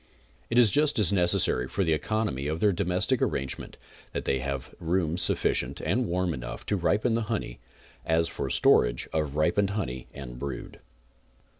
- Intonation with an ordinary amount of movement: No, wide, 6.6 semitones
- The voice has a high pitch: No, very low, 85 Hz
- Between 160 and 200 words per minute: Yes, average, 165 wpm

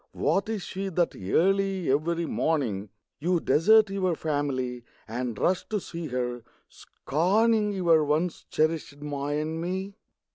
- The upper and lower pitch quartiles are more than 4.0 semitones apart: Yes, average, 4.8 semitones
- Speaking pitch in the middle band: Yes, medium, 165 Hz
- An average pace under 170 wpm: Yes, slow, 135 wpm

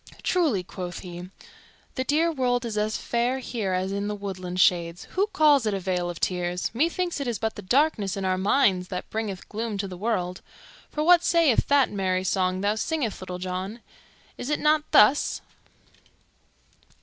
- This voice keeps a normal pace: Yes, average, 180 wpm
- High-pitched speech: Yes, high, 210 Hz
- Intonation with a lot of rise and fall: Yes, wide, 6.3 semitones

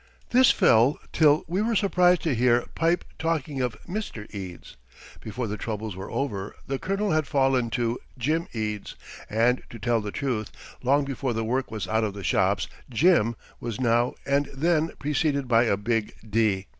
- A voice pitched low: Yes, low, 125 Hz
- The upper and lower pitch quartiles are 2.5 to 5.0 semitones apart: No, wide, 5.4 semitones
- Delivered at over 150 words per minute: Yes, average, 175 wpm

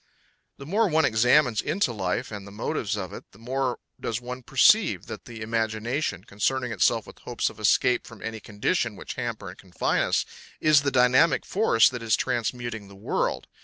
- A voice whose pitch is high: No, low, 120 Hz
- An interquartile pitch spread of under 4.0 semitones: Yes, average, 3.4 semitones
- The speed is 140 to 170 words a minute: No, average, 185 wpm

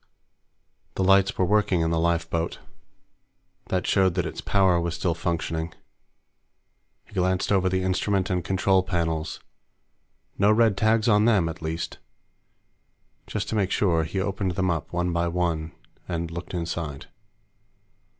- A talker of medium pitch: No, very low, 90 Hz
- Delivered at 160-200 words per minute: No, average, 145 wpm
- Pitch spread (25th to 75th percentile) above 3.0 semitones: No, narrow, 2.5 semitones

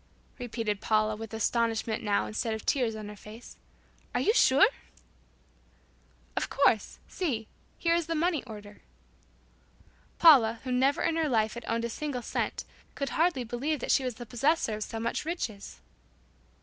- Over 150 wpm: Yes, average, 160 wpm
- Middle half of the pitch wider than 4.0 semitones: Yes, average, 4.7 semitones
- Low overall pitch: No, high, 235 Hz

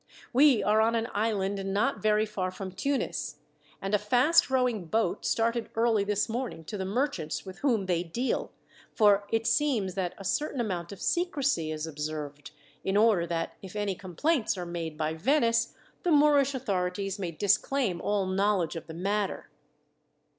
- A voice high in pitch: Yes, high, 205 Hz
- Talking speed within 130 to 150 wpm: No, average, 170 wpm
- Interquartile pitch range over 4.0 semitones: Yes, average, 4.5 semitones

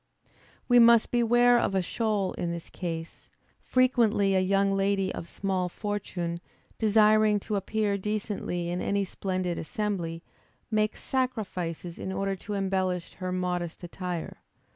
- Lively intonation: No, average, 3.0 semitones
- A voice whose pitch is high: Yes, high, 195 Hz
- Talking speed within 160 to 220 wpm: No, slow, 135 wpm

